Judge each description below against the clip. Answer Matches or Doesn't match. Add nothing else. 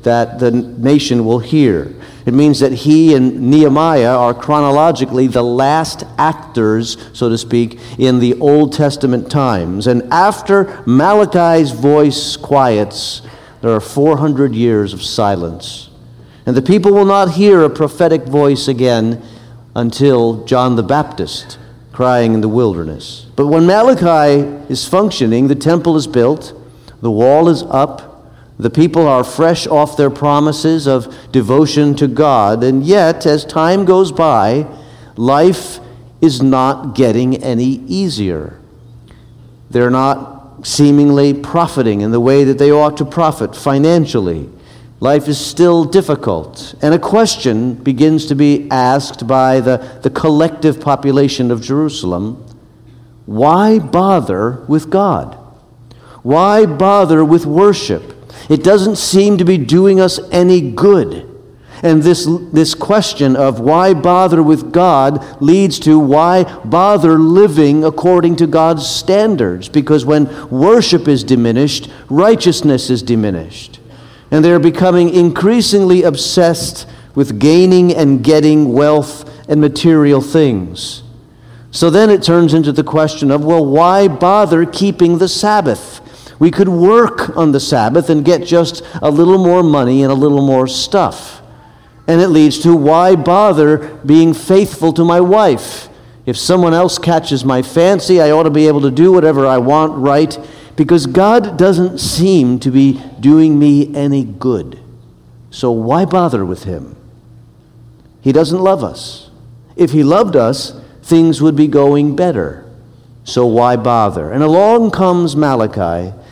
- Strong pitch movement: Doesn't match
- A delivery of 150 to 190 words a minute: Doesn't match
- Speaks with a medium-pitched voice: Matches